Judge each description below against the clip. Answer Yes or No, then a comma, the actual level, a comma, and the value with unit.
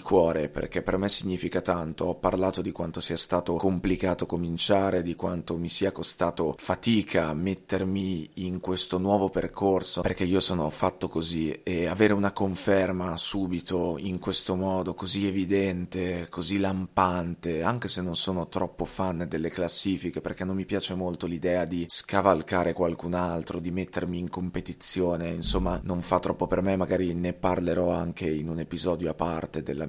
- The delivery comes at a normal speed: Yes, average, 160 wpm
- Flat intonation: Yes, narrow, 1.7 semitones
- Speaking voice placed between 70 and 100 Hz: Yes, very low, 90 Hz